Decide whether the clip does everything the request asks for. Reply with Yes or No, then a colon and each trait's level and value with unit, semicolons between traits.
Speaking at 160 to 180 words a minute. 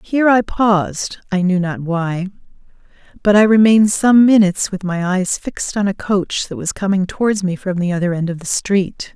No: fast, 205 wpm